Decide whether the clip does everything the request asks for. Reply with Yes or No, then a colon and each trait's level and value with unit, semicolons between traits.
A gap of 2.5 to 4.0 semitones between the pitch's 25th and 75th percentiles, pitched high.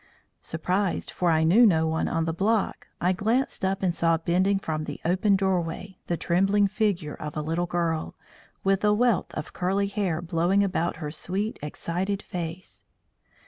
No: average, 3.3 semitones; medium, 180 Hz